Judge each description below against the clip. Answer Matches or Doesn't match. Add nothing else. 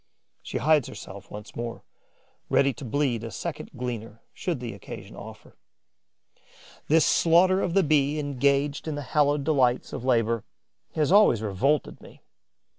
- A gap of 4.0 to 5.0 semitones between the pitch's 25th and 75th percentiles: Matches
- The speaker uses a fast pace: Doesn't match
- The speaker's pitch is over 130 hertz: Matches